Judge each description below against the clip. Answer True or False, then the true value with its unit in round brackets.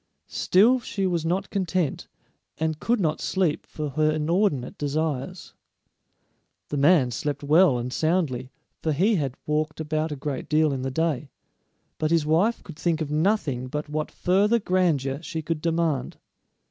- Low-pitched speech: False (155 Hz)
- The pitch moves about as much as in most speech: True (3.5 semitones)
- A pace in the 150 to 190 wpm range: True (160 wpm)